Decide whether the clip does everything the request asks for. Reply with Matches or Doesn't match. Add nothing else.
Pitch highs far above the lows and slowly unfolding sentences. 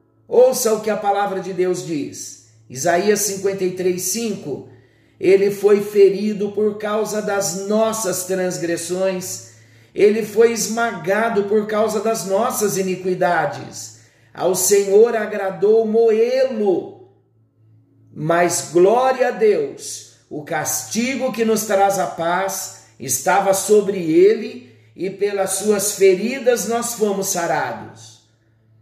Doesn't match